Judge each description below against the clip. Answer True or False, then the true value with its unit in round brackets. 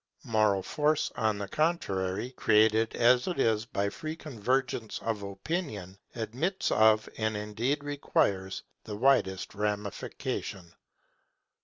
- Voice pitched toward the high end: False (110 Hz)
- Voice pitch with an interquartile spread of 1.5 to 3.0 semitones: False (4.7 semitones)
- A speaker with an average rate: False (115 wpm)